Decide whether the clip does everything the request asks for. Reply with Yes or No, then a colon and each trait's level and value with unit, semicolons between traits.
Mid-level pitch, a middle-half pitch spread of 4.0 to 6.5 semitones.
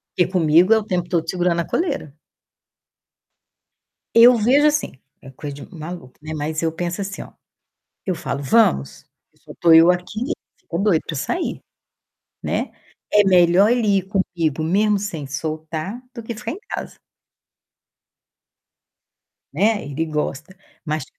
Yes: medium, 175 Hz; average, 4.9 semitones